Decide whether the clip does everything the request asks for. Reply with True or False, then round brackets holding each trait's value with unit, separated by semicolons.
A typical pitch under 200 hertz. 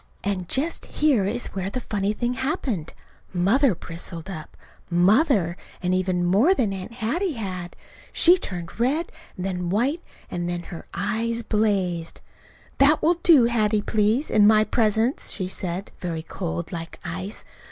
False (205 Hz)